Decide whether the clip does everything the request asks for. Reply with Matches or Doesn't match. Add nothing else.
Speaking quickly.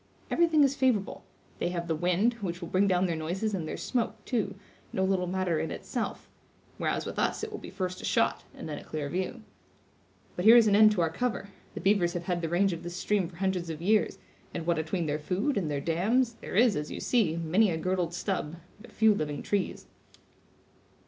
Matches